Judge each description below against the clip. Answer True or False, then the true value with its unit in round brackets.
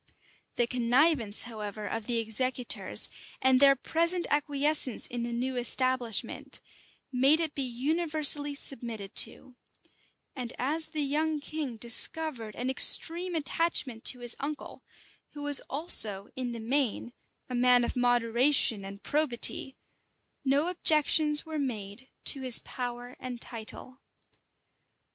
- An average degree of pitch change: True (3.8 semitones)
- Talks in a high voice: True (255 Hz)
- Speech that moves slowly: True (125 wpm)